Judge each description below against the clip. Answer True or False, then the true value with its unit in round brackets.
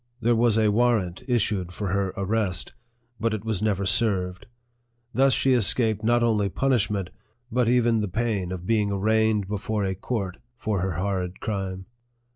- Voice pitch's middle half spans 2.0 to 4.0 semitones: True (3.1 semitones)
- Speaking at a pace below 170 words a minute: True (160 wpm)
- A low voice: True (105 Hz)